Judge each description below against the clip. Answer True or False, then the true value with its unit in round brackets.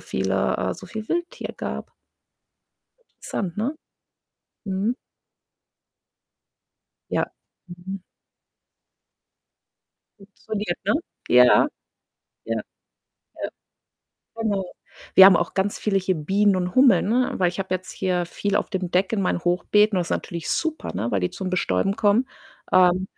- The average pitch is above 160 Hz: True (190 Hz)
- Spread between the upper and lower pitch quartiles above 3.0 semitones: False (2.7 semitones)